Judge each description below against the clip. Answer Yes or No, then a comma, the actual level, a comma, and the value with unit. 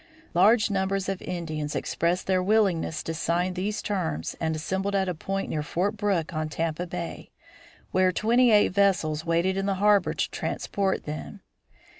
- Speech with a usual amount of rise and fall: Yes, average, 3.3 semitones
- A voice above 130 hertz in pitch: Yes, medium, 185 Hz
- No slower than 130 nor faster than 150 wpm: No, average, 165 wpm